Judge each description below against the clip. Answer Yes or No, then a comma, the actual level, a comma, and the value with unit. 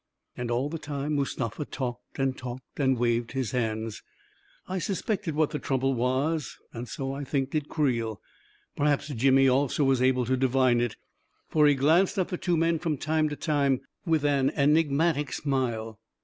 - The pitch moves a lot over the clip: No, average, 3.1 semitones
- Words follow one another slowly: No, average, 175 wpm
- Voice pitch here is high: No, low, 135 Hz